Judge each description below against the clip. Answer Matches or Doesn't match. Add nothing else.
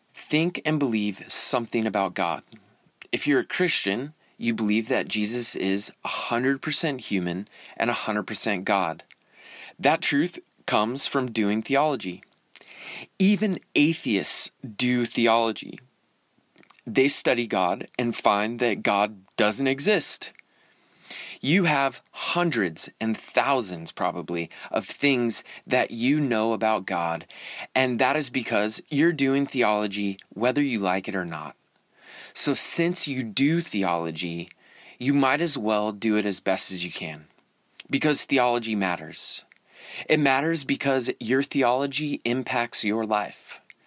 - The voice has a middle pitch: Doesn't match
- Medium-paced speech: Doesn't match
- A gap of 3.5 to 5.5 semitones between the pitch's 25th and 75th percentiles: Matches